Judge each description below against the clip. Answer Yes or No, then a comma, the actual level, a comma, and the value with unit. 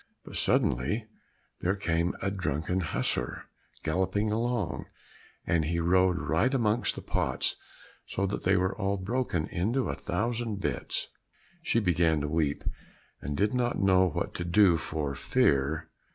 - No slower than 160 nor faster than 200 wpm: No, average, 145 wpm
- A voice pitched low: Yes, very low, 95 Hz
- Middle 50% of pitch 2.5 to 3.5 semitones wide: No, average, 4.6 semitones